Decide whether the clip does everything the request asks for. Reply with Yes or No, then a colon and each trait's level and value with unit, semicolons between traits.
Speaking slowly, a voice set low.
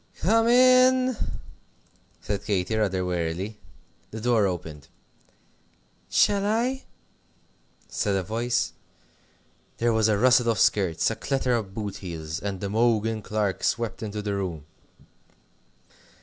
Yes: slow, 120 wpm; low, 110 Hz